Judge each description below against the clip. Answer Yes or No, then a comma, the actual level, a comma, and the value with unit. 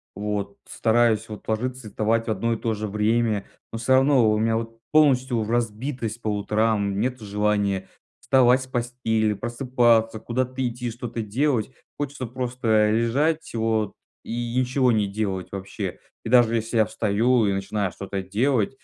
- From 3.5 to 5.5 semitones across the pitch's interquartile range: No, average, 2.8 semitones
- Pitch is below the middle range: Yes, low, 115 Hz